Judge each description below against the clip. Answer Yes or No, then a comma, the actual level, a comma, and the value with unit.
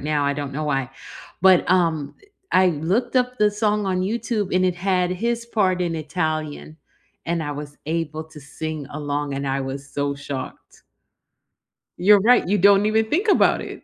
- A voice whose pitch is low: No, medium, 170 Hz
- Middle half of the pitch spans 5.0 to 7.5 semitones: Yes, wide, 5.5 semitones